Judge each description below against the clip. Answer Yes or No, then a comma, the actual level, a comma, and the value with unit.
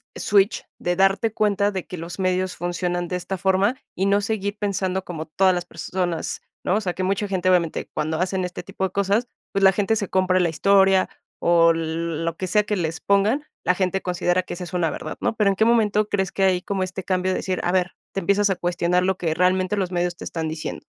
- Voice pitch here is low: No, medium, 185 Hz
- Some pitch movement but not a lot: No, narrow, 1.9 semitones